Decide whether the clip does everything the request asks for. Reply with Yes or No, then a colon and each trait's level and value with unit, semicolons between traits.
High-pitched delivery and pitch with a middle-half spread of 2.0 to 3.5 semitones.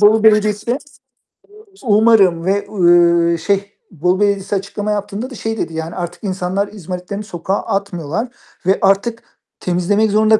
Yes: high, 200 Hz; average, 2.9 semitones